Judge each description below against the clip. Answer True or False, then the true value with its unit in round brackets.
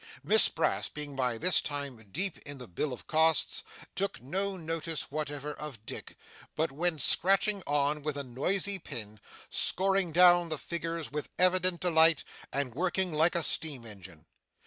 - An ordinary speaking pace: True (160 wpm)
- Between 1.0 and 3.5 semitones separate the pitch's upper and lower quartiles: False (4.0 semitones)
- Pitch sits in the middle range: True (155 Hz)